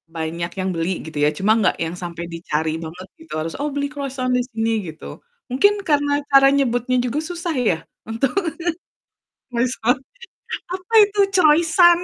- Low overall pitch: No, high, 245 Hz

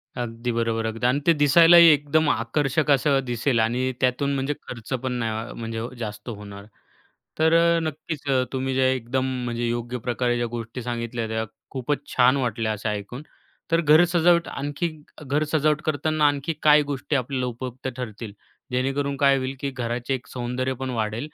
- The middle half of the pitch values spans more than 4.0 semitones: No, average, 3.7 semitones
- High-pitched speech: No, low, 130 Hz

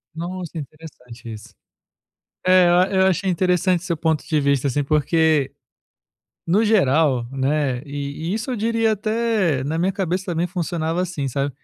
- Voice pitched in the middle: Yes, medium, 165 Hz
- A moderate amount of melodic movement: Yes, average, 4.6 semitones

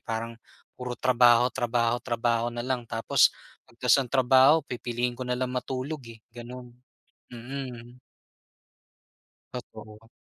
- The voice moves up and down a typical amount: No, narrow, 1.4 semitones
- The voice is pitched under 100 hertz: No, low, 120 Hz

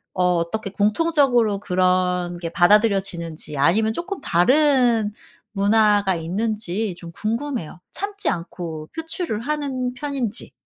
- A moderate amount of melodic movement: No, wide, 6.0 semitones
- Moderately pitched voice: No, high, 210 Hz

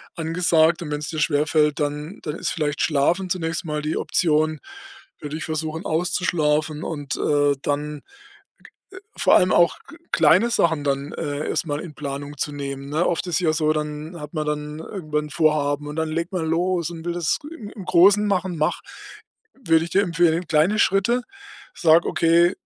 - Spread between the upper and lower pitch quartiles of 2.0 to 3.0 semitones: Yes, narrow, 2.5 semitones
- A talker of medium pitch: Yes, medium, 160 Hz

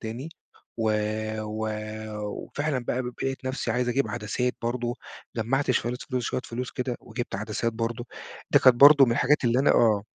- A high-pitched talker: No, low, 120 Hz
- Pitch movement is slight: Yes, narrow, 2.1 semitones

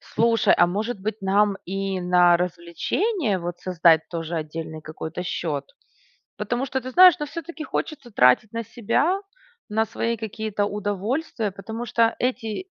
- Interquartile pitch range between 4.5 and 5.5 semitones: Yes, average, 4.9 semitones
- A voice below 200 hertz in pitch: No, high, 205 Hz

